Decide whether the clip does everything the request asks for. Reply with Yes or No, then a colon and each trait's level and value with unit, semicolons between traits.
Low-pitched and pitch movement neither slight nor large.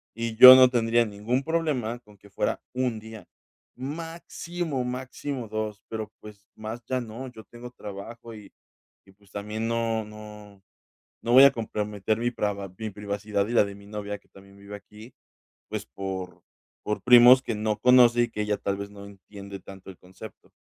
Yes: low, 110 Hz; average, 3.0 semitones